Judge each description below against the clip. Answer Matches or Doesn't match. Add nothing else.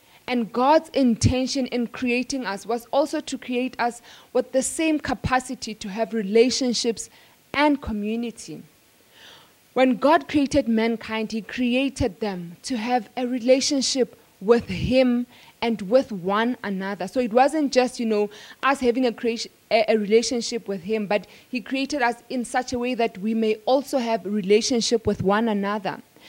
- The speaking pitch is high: Matches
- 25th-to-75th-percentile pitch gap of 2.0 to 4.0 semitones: Matches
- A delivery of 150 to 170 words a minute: Matches